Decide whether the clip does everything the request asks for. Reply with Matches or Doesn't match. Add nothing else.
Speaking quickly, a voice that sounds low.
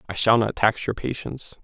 Matches